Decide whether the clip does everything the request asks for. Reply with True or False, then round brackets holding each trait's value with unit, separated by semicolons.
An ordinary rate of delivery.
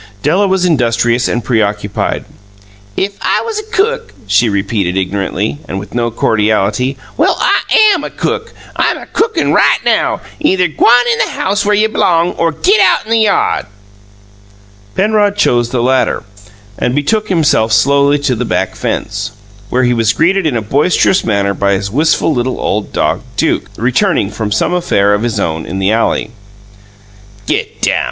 True (170 wpm)